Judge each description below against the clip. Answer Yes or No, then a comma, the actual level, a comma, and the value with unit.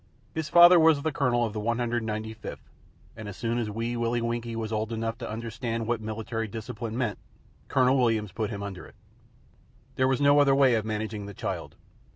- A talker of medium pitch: No, low, 115 Hz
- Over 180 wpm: Yes, average, 190 wpm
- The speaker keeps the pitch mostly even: Yes, narrow, 2.2 semitones